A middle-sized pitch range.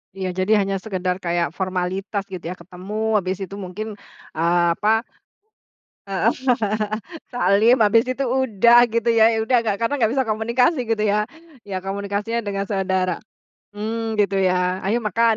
Yes: average, 3.2 semitones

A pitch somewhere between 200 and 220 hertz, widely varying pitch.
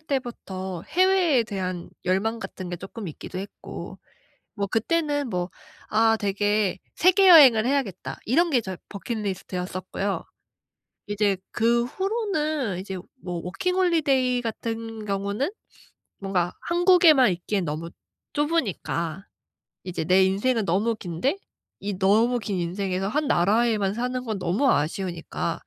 Yes: high, 210 Hz; wide, 5.7 semitones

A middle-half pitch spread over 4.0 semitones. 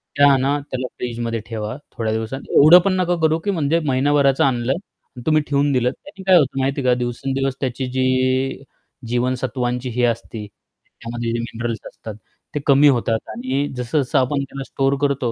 No: average, 2.7 semitones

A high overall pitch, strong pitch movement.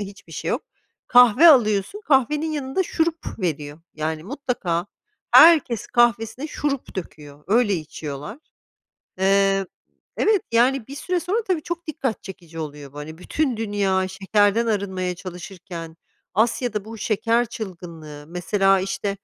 Yes: high, 205 Hz; wide, 6.2 semitones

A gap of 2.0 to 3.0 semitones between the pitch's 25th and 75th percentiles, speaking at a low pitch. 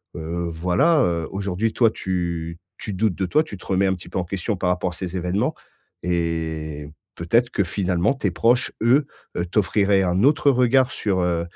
No: average, 4.0 semitones; very low, 95 Hz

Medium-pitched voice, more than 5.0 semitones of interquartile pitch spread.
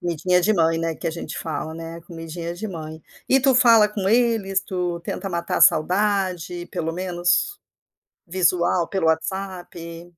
No: medium, 175 Hz; average, 2.8 semitones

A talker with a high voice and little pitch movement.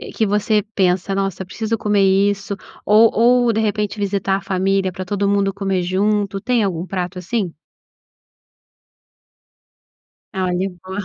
Yes: high, 195 Hz; narrow, 1.8 semitones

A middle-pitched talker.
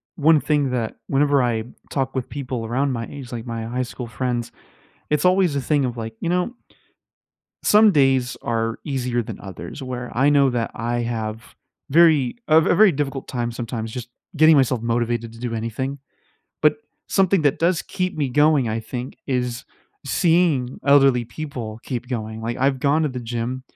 No: low, 130 Hz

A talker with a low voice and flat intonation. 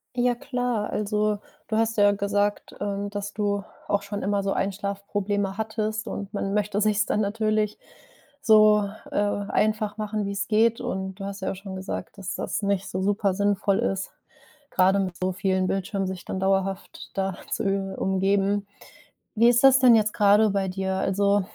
No: high, 200 Hz; narrow, 1.6 semitones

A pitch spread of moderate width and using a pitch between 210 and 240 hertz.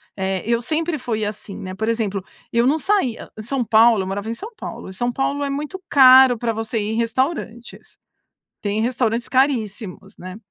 Yes: average, 3.6 semitones; high, 235 Hz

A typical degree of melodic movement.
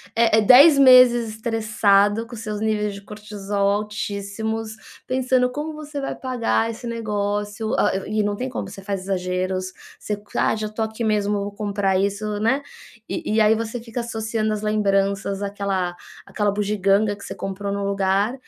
No: narrow, 2.1 semitones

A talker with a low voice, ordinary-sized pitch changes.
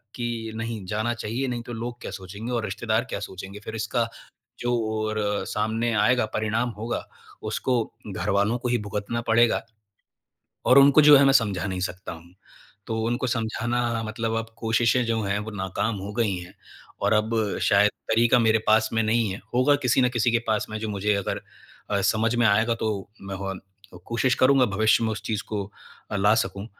No: low, 110 Hz; narrow, 2.3 semitones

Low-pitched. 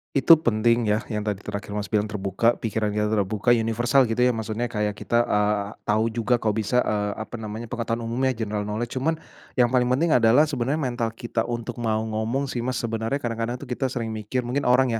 Yes: low, 115 Hz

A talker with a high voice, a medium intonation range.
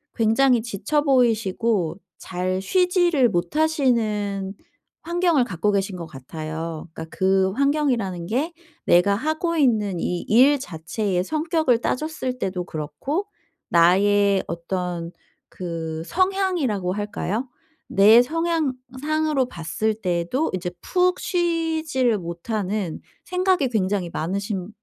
No: high, 215 Hz; wide, 8.2 semitones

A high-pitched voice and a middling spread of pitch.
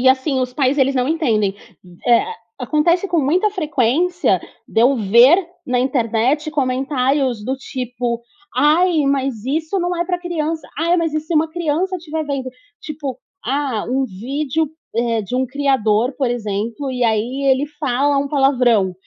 Yes: very high, 270 Hz; average, 4.0 semitones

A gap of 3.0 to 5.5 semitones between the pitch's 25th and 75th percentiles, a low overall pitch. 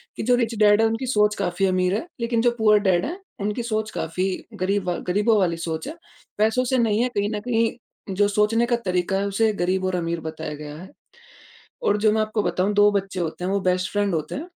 No: average, 3.4 semitones; high, 205 Hz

